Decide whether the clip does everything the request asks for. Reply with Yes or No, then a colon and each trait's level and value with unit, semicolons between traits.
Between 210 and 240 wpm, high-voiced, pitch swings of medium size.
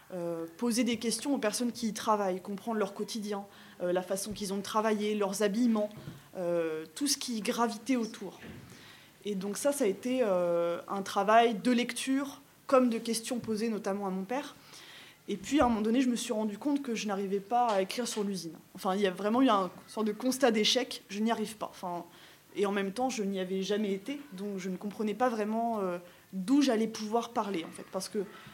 Yes: fast, 220 wpm; high, 210 Hz; average, 3.6 semitones